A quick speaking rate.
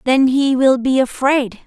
No: average, 180 wpm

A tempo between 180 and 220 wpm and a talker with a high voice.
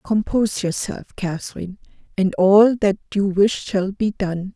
No: average, 145 wpm; high, 195 Hz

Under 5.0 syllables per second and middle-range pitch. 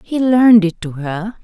No: 4.5 syllables/s; high, 205 Hz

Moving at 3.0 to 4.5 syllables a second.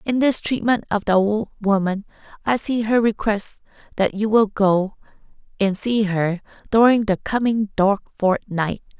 Yes: 4.3 syllables/s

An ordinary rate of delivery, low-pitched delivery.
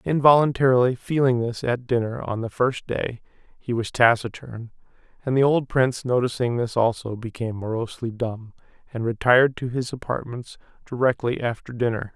Yes: average, 150 wpm; low, 120 Hz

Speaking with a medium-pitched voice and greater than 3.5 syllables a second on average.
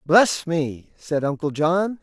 No: medium, 165 Hz; 3.3 syllables/s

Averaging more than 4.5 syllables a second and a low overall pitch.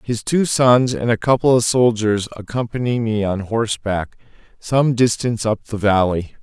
Yes: 4.7 syllables/s; low, 115 Hz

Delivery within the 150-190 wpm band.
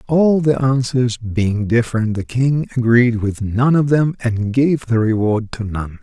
Yes: average, 180 wpm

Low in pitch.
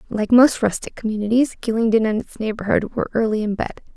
No: high, 220 Hz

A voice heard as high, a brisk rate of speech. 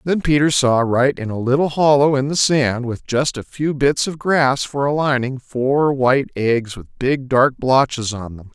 No: low, 135 Hz; fast, 210 wpm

